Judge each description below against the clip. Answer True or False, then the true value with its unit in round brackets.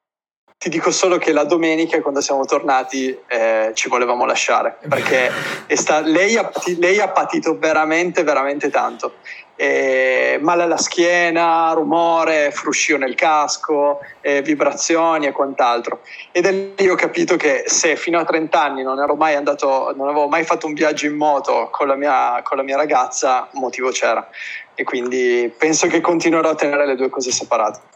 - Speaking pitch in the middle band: True (155 Hz)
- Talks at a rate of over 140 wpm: True (165 wpm)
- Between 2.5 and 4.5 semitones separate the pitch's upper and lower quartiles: True (3.4 semitones)